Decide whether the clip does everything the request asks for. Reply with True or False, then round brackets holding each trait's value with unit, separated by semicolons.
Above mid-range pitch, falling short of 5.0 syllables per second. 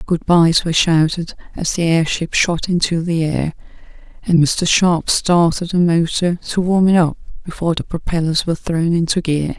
False (165 Hz; 4.8 syllables/s)